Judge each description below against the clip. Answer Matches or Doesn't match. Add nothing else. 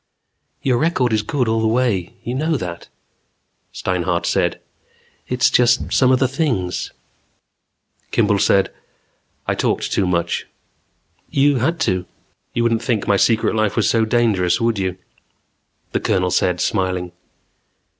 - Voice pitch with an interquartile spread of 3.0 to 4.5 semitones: Doesn't match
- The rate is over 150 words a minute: Doesn't match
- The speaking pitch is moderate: Doesn't match